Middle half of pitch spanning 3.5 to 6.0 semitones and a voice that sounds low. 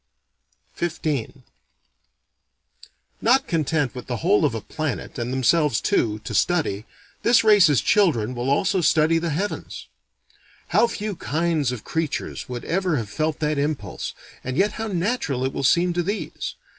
No: wide, 5.5 semitones; medium, 155 Hz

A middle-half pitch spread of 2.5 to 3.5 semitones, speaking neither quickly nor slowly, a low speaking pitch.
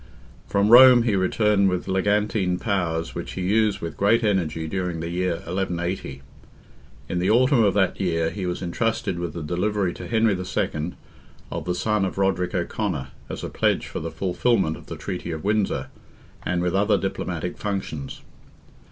Yes: average, 3.1 semitones; average, 170 wpm; very low, 95 Hz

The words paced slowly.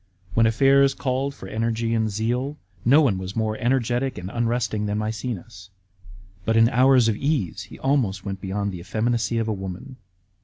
No: average, 170 wpm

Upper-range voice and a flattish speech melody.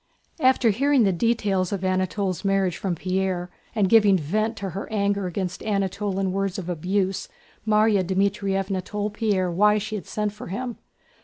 Yes: high, 195 Hz; narrow, 2.1 semitones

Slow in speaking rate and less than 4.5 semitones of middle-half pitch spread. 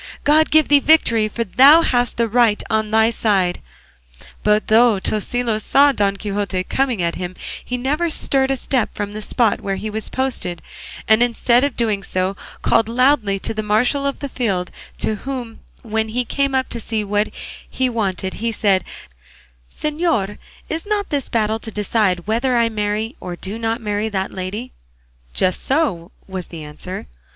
No: average, 180 wpm; average, 3.9 semitones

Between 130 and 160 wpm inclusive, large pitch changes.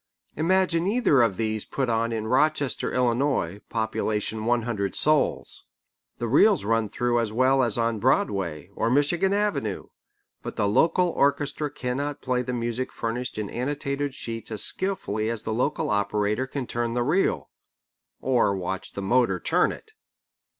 No: average, 155 wpm; average, 4.6 semitones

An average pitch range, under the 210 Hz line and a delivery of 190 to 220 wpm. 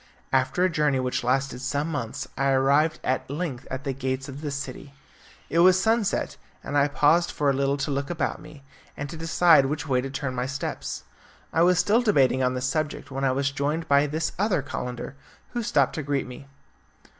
Yes: average, 3.0 semitones; medium, 140 Hz; fast, 205 wpm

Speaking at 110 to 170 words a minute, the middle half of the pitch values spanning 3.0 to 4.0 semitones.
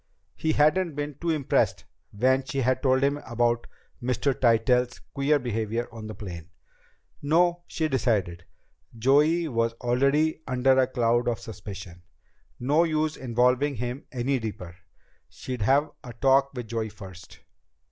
Yes: average, 140 wpm; average, 3.7 semitones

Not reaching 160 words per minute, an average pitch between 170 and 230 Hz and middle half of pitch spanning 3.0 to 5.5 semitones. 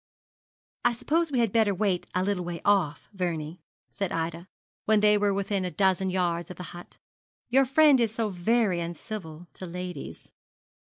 No: average, 170 wpm; high, 190 Hz; average, 3.7 semitones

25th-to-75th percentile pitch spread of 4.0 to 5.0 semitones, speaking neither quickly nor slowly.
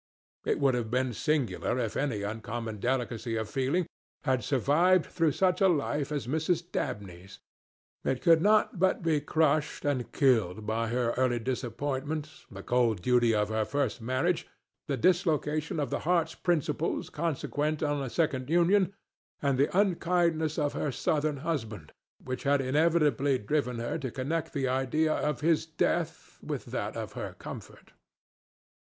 Yes: average, 4.6 semitones; average, 155 wpm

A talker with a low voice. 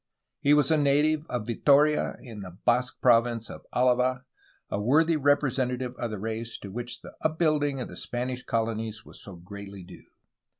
Yes: low, 125 Hz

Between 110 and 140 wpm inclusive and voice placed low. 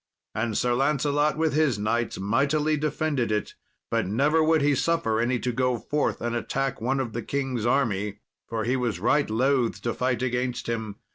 No: average, 185 wpm; low, 125 Hz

